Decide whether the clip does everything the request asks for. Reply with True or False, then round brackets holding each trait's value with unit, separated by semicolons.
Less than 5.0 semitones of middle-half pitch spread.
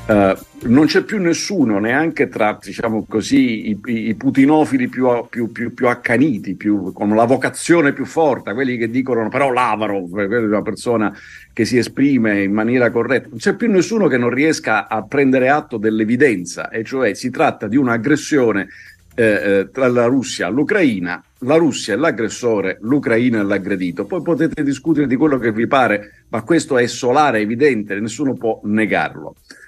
False (5.3 semitones)